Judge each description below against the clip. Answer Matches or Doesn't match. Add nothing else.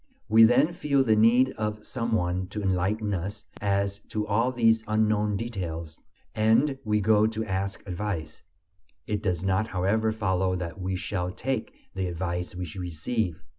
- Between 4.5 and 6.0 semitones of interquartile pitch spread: Doesn't match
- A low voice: Matches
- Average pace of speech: Matches